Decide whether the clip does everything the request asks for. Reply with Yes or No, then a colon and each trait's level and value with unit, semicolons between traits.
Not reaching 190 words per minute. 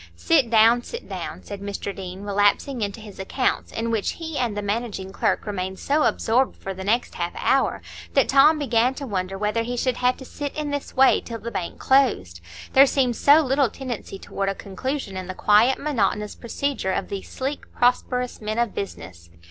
No: average, 195 wpm